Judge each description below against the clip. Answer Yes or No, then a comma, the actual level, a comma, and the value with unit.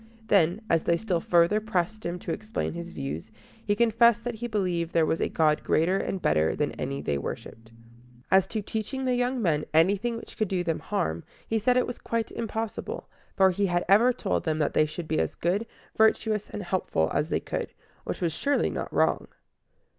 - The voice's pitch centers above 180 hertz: Yes, high, 190 Hz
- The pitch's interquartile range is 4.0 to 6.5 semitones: Yes, average, 5.1 semitones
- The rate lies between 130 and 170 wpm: No, fast, 205 wpm